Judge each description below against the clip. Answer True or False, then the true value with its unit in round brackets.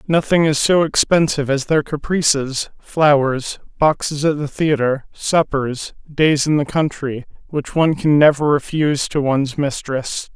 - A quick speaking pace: False (145 wpm)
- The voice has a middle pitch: True (145 Hz)